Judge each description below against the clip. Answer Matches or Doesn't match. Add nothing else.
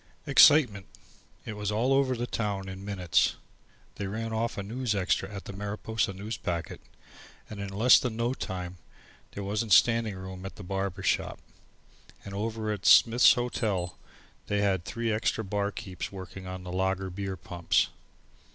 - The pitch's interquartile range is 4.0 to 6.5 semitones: Doesn't match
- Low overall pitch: Matches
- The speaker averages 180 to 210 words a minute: Doesn't match